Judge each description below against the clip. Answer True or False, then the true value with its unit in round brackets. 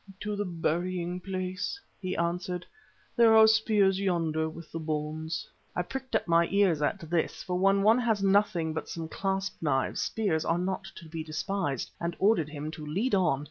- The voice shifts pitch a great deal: False (3.6 semitones)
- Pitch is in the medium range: True (180 Hz)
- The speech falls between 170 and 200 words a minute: True (180 wpm)